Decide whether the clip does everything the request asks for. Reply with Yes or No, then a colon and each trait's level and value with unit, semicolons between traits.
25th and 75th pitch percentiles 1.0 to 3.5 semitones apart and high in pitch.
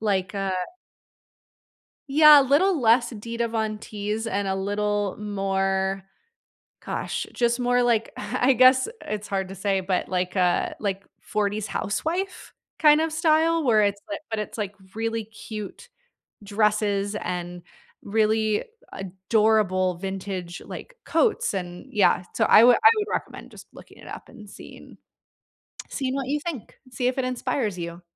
No: average, 4.2 semitones; high, 210 Hz